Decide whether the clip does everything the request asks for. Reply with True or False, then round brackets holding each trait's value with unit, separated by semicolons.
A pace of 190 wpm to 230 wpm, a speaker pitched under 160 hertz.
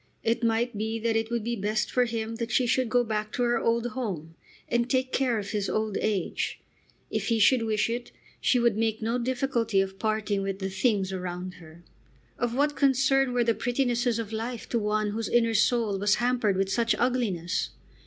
False (205 wpm; 225 Hz)